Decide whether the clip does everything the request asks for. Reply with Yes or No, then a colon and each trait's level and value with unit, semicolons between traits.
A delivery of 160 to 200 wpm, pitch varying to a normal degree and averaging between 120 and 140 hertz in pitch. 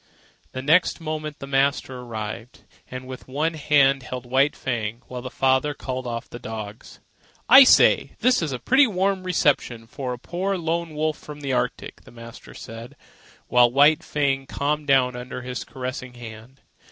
Yes: average, 170 wpm; average, 3.6 semitones; low, 135 Hz